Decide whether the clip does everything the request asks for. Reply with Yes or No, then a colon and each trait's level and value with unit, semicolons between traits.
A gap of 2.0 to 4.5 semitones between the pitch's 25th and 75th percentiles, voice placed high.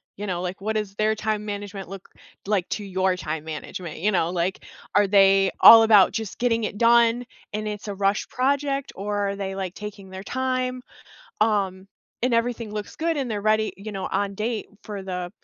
Yes: narrow, 2.5 semitones; high, 205 Hz